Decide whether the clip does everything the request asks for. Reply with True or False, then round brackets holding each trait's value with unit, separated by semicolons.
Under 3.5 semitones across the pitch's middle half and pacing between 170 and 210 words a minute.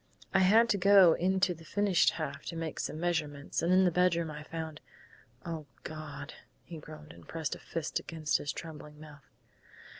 True (2.9 semitones; 180 wpm)